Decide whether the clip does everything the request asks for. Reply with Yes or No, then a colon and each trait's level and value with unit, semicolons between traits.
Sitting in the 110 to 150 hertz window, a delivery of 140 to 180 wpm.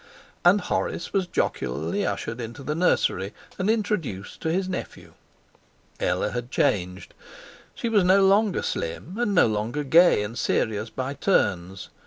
Yes: medium, 140 Hz; average, 145 wpm